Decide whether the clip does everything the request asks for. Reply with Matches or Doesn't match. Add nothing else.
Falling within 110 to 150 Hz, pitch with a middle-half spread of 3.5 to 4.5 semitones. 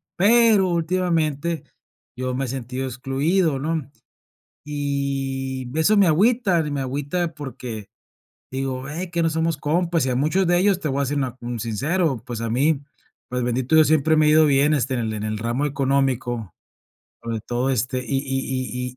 Matches